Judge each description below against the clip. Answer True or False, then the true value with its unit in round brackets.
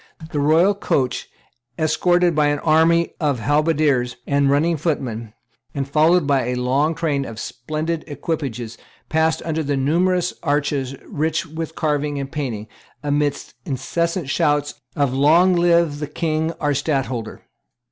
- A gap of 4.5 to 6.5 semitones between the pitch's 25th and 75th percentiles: False (2.8 semitones)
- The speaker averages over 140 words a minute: False (135 wpm)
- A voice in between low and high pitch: True (150 Hz)